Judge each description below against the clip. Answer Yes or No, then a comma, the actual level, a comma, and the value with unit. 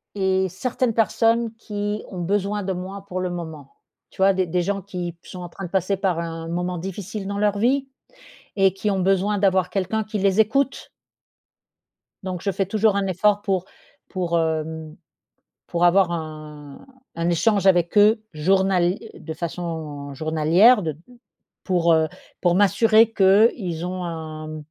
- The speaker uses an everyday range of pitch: Yes, average, 3.2 semitones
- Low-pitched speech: No, medium, 185 Hz